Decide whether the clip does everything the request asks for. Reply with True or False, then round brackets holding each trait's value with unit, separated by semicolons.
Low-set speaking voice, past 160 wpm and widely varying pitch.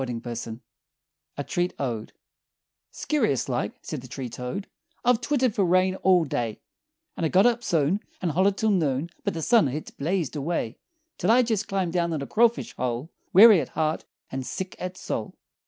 False (170 Hz; 175 wpm; 6.8 semitones)